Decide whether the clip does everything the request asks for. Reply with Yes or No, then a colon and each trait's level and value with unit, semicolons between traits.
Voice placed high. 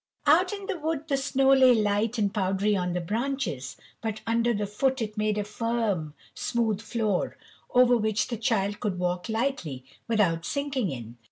Yes: high, 215 Hz